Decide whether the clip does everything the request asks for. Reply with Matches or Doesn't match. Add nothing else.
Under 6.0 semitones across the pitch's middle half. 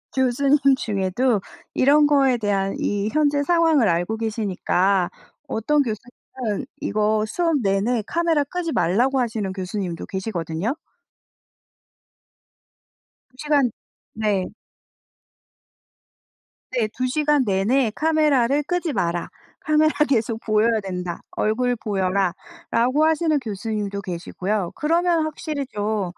Doesn't match